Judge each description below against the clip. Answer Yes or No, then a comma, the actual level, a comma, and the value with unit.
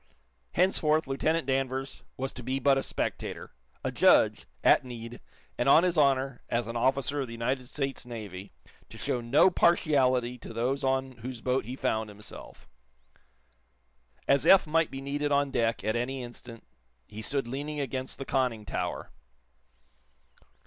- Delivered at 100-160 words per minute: Yes, average, 155 wpm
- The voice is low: Yes, low, 130 Hz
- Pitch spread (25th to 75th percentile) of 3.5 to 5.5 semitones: No, average, 2.7 semitones